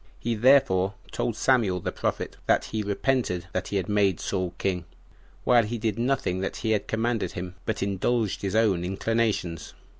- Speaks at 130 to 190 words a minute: Yes, average, 175 wpm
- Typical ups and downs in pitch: Yes, average, 3.8 semitones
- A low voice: Yes, low, 105 Hz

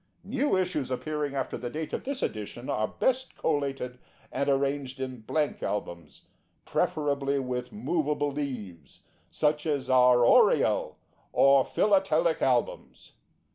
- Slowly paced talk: Yes, slow, 125 wpm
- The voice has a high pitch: No, medium, 140 Hz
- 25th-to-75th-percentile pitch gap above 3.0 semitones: Yes, average, 3.5 semitones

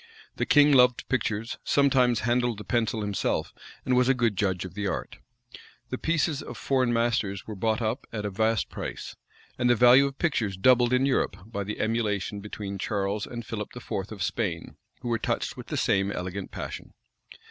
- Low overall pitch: Yes, low, 115 Hz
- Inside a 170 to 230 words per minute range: Yes, average, 190 wpm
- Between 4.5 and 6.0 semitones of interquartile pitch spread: No, average, 3.5 semitones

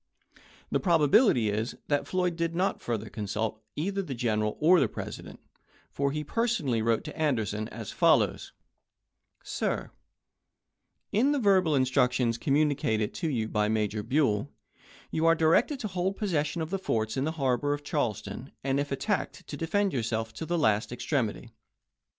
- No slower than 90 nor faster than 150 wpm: No, average, 160 wpm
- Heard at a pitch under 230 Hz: Yes, medium, 140 Hz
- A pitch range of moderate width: No, wide, 6.9 semitones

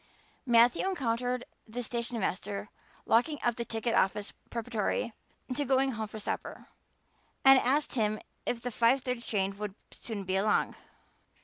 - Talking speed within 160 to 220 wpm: No, average, 140 wpm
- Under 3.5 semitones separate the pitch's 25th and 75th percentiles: Yes, average, 2.8 semitones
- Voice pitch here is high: Yes, high, 235 Hz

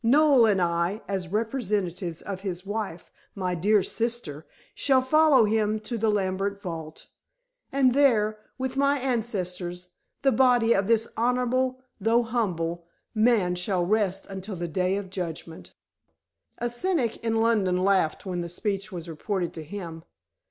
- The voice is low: No, high, 205 Hz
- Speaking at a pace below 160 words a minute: Yes, average, 145 wpm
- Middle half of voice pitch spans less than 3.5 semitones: No, average, 4.6 semitones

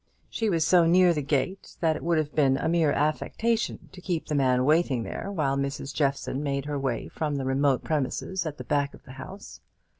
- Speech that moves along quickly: Yes, fast, 215 wpm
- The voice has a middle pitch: Yes, medium, 150 Hz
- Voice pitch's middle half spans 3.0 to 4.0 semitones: Yes, average, 3.6 semitones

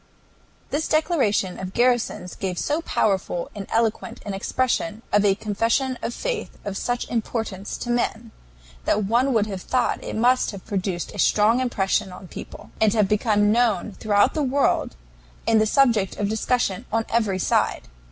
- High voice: Yes, high, 220 Hz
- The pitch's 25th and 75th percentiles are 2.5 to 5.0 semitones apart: Yes, average, 3.4 semitones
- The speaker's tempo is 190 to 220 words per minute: No, average, 165 wpm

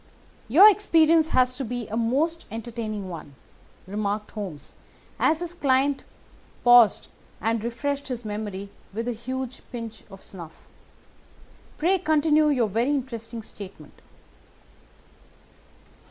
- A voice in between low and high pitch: No, high, 240 Hz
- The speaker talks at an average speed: No, slow, 110 wpm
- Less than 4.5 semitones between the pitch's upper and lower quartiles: No, average, 5.1 semitones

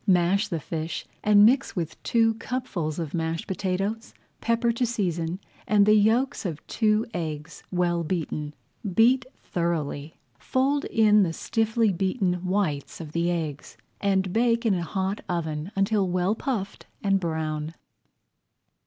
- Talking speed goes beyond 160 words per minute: No, average, 140 wpm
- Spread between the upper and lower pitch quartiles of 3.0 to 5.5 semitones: Yes, average, 4.8 semitones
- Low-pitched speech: No, high, 190 Hz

